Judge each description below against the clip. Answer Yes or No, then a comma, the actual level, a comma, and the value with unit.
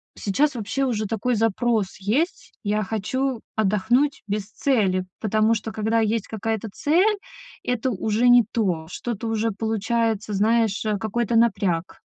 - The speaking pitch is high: Yes, high, 220 Hz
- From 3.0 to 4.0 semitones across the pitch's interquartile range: No, narrow, 2.4 semitones